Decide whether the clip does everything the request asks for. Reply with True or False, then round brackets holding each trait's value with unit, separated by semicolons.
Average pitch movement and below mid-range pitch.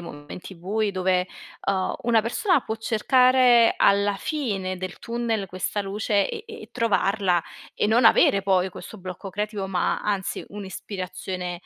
False (3.4 semitones; 200 Hz)